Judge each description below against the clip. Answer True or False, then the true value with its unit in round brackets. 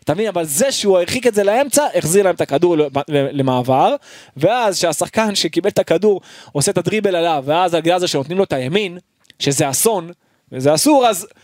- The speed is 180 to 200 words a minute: True (190 wpm)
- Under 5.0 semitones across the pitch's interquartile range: False (5.5 semitones)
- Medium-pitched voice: True (180 Hz)